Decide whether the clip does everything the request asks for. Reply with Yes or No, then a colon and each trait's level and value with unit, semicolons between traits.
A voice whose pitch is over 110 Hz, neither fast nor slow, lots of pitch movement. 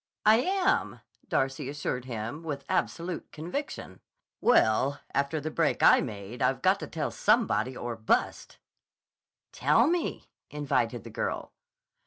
No: medium, 140 Hz; slow, 130 wpm; wide, 6.9 semitones